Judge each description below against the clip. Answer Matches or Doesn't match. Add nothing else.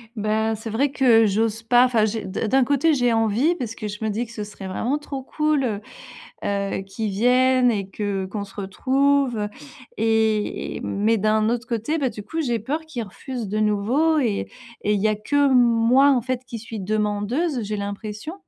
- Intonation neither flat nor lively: Matches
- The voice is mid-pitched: Doesn't match